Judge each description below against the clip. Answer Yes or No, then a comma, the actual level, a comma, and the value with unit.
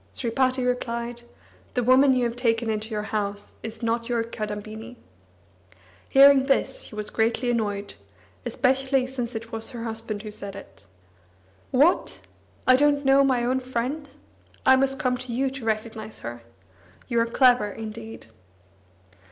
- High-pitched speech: Yes, high, 235 Hz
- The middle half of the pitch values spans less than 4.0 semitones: Yes, average, 2.8 semitones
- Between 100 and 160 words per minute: Yes, average, 150 wpm